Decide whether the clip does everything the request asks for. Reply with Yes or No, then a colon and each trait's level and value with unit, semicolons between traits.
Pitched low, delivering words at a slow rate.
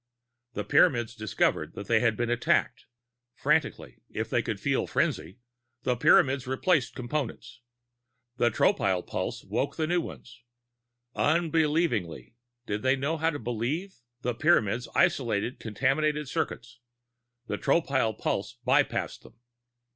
Yes: low, 125 Hz; slow, 125 wpm